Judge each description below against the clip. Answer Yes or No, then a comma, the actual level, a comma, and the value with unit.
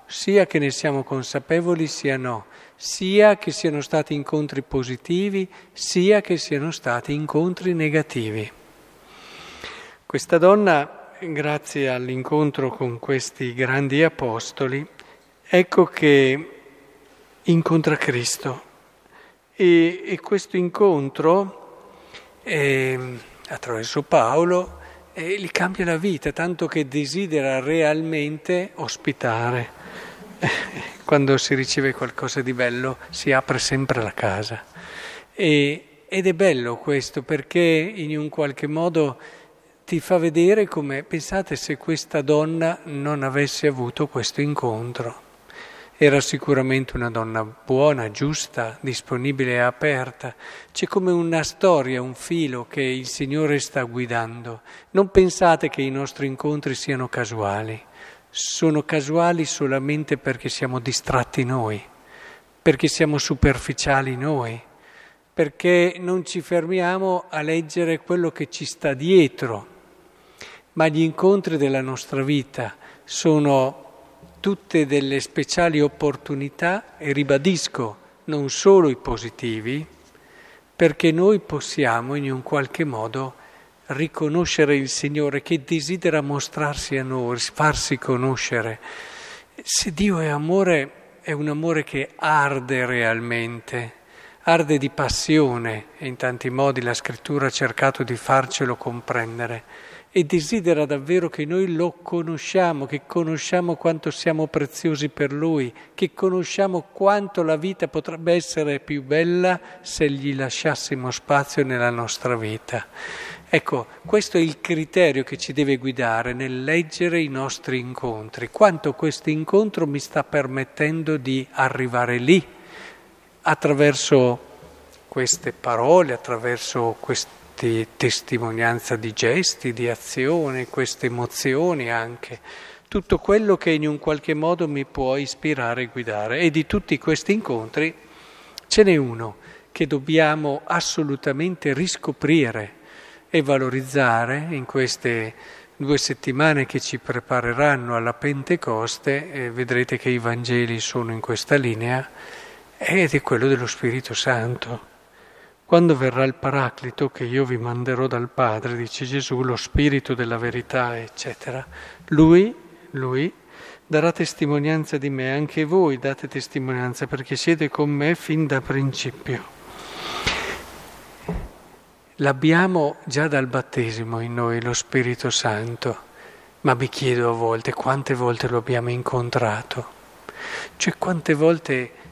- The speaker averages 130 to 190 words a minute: No, average, 120 wpm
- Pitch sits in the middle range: Yes, medium, 145 Hz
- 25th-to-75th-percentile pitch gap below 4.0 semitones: No, average, 4.3 semitones